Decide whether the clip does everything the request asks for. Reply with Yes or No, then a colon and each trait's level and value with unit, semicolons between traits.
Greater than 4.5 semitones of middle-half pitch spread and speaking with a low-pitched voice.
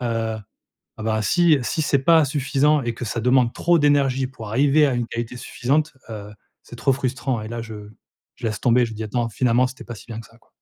No: average, 3.3 semitones; low, 125 Hz